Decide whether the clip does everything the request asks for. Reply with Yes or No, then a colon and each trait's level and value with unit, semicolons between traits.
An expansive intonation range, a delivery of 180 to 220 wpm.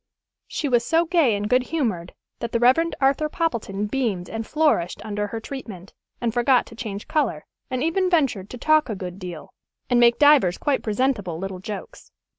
Yes: wide, 6.0 semitones; average, 185 wpm